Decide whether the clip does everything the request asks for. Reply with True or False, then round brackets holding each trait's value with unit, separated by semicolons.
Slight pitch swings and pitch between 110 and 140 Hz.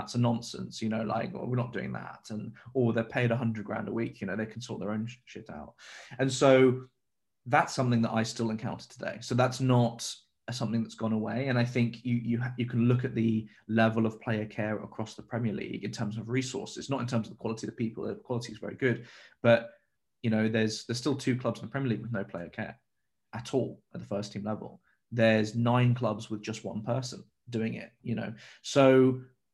True (2.1 semitones; 115 Hz)